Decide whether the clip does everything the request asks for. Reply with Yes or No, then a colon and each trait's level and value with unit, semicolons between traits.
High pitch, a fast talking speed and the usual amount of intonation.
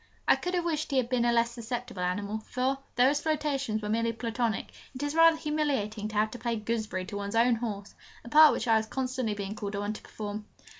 Yes: high, 230 Hz; fast, 235 wpm; average, 4.0 semitones